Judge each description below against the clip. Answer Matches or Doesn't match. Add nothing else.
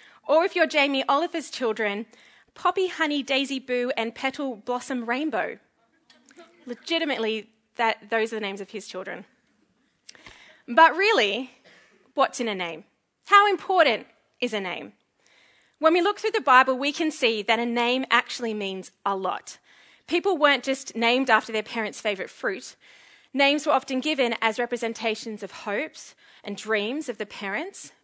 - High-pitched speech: Matches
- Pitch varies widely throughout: Matches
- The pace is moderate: Matches